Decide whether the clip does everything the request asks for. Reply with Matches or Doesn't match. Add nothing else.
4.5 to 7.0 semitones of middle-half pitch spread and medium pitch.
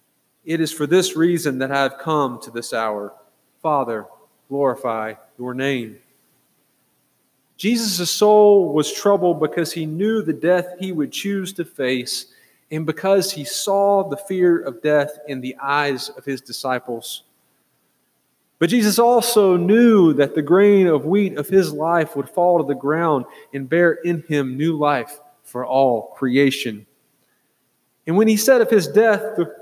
Matches